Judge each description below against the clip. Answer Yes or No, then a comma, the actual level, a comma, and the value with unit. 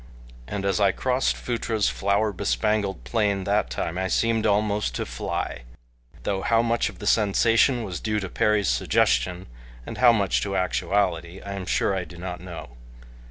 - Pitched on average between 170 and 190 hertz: No, low, 100 Hz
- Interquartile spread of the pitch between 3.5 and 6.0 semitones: No, average, 2.8 semitones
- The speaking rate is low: No, average, 170 wpm